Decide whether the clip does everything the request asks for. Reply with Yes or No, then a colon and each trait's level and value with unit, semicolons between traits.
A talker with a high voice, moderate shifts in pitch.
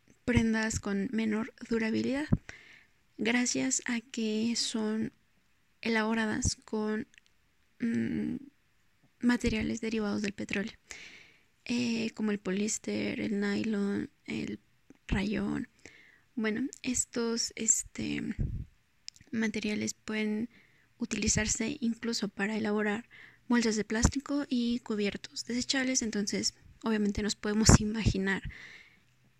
No: high, 225 Hz; narrow, 2.2 semitones